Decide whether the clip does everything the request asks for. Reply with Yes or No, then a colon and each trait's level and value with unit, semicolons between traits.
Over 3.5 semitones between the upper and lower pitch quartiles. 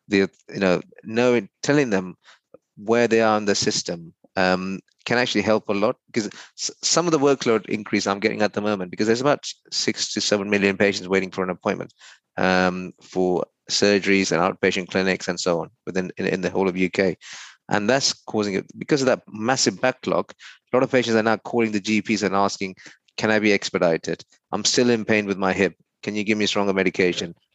No: average, 2.8 semitones